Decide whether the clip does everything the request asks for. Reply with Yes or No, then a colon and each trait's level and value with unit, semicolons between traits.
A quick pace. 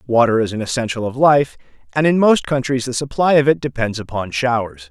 Yes: fast, 210 wpm